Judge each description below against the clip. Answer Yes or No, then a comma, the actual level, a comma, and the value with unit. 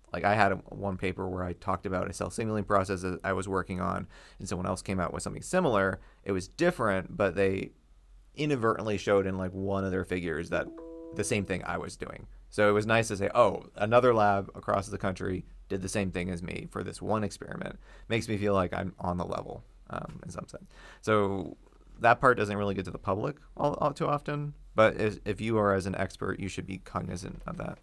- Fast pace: Yes, fast, 230 wpm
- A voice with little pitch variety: Yes, narrow, 2.0 semitones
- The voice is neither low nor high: No, low, 100 Hz